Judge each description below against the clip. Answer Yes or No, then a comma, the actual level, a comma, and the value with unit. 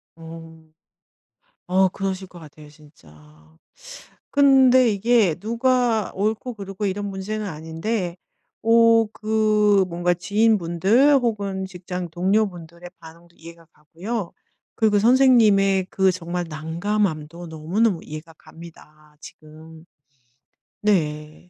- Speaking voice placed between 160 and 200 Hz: Yes, medium, 185 Hz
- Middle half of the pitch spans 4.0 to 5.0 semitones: Yes, average, 4.7 semitones